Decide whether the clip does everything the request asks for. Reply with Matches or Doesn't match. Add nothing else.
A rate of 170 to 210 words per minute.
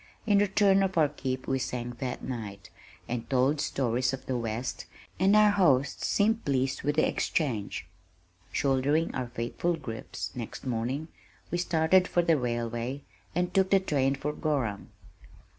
Doesn't match